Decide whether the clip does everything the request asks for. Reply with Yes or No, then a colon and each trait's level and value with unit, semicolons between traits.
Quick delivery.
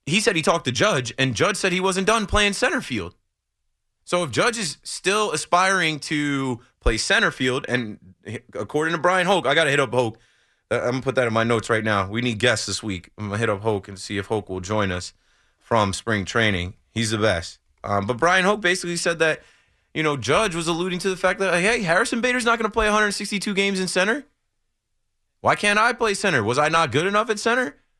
Yes: fast, 225 wpm